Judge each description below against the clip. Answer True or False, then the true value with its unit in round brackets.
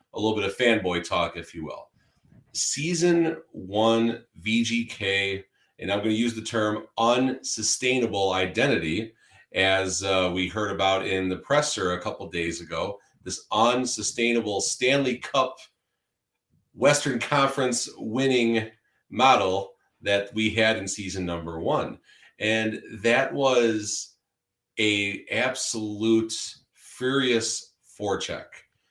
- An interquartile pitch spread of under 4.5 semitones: True (3.6 semitones)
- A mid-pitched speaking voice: False (110 Hz)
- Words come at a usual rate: False (115 wpm)